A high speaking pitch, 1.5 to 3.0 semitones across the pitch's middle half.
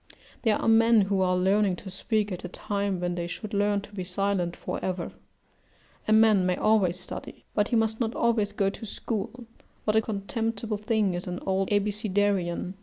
Yes: high, 205 Hz; average, 2.7 semitones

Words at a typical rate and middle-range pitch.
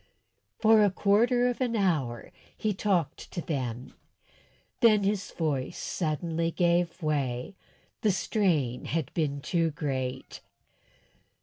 No: slow, 115 wpm; medium, 170 Hz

